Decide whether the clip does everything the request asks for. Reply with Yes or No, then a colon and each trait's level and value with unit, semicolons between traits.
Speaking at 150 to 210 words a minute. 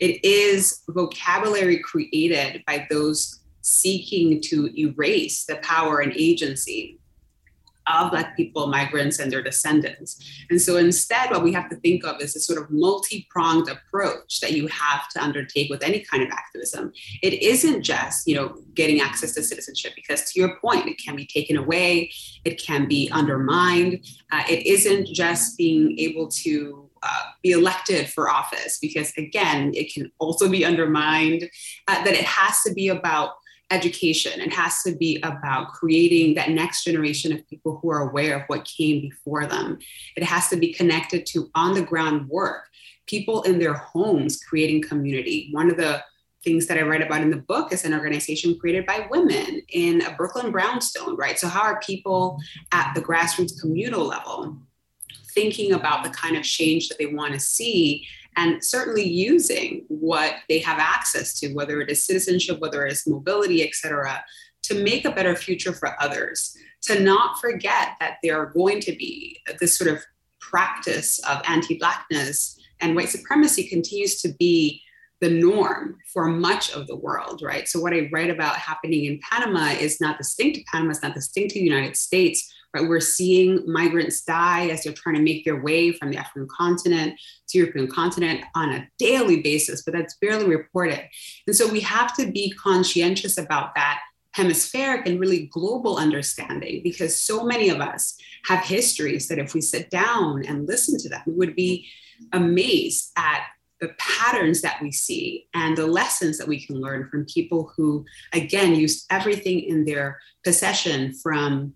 Yes: average, 175 wpm